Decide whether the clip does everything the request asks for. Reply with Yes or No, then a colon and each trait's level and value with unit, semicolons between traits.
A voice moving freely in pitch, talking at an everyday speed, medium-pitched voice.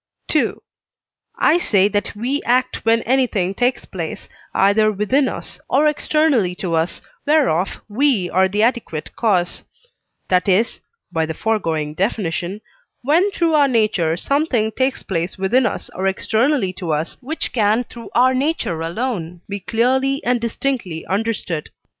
No: wide, 6.0 semitones; average, 145 wpm; high, 215 Hz